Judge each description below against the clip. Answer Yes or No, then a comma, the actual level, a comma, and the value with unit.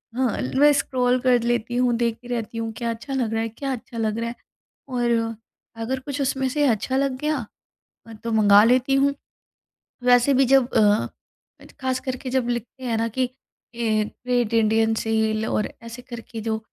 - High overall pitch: Yes, high, 240 Hz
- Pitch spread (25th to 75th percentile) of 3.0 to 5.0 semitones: No, narrow, 2.4 semitones